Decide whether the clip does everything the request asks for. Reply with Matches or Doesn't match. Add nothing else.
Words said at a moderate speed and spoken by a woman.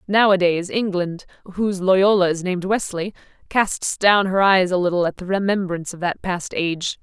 Matches